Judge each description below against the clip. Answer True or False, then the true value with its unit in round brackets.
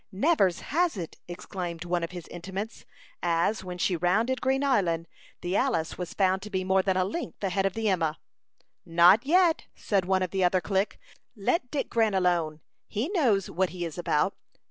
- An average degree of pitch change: True (3.8 semitones)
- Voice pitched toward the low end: False (190 Hz)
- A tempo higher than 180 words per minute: True (190 wpm)